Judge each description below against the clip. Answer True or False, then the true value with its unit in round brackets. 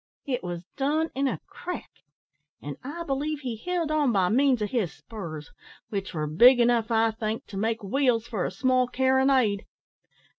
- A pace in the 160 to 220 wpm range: True (175 wpm)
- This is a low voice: False (240 Hz)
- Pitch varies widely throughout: False (4.7 semitones)